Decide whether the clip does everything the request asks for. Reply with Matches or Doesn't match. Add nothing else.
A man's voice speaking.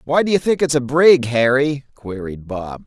Matches